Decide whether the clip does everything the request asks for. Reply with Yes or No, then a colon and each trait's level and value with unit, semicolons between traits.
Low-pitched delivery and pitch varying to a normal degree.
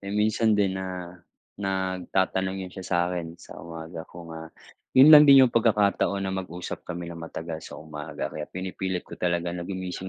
No: very low, 95 Hz; narrow, 2.1 semitones